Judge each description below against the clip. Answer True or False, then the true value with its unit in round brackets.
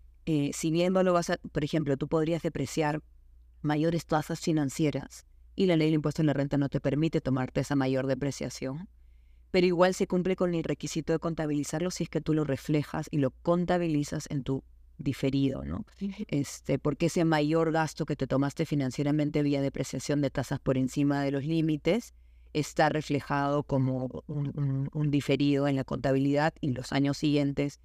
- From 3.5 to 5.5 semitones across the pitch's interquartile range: False (2.7 semitones)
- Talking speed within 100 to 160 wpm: False (180 wpm)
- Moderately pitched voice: True (145 Hz)